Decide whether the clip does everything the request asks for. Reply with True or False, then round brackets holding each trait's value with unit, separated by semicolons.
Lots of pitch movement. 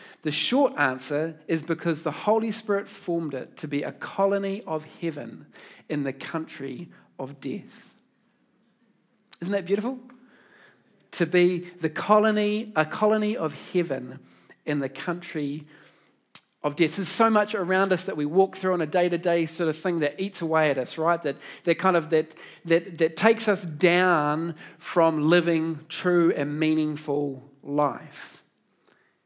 False (4.3 semitones)